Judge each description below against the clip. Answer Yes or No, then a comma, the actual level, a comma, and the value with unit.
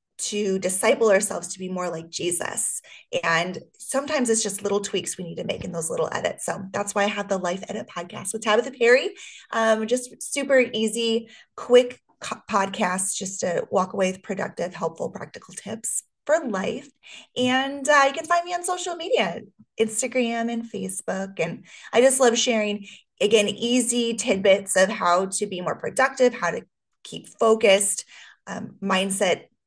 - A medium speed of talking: Yes, average, 170 wpm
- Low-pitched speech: No, high, 220 Hz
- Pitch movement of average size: Yes, average, 4.4 semitones